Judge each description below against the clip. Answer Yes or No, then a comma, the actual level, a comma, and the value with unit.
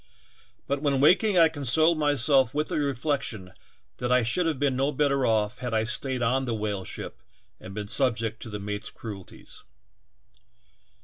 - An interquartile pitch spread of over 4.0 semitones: Yes, average, 4.5 semitones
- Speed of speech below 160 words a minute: No, average, 175 wpm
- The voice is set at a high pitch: No, low, 130 Hz